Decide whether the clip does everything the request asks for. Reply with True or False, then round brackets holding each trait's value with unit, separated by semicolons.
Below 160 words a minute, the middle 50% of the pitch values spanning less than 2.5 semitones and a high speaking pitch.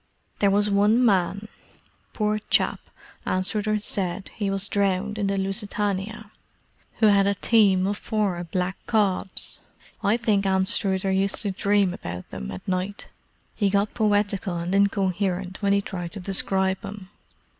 True (140 wpm; 1.6 semitones; 200 Hz)